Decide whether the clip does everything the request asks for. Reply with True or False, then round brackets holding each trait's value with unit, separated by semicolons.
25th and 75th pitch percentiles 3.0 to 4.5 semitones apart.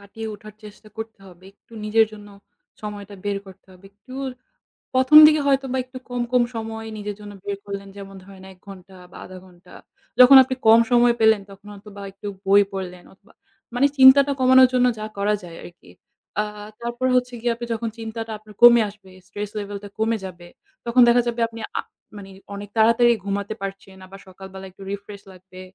True (3.3 semitones)